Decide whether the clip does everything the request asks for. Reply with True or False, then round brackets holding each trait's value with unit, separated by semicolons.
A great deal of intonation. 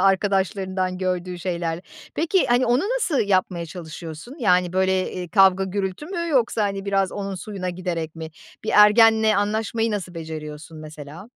False (3.2 semitones)